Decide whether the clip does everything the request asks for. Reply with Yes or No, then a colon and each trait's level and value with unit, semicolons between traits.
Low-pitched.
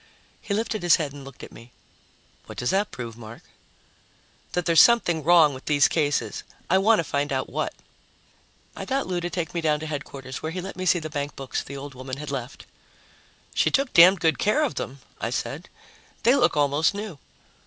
No: medium, 155 Hz